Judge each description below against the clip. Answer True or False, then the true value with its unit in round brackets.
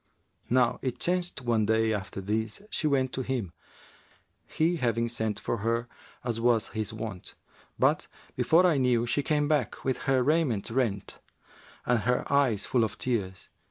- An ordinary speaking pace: True (160 wpm)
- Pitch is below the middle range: True (120 Hz)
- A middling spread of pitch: True (3.3 semitones)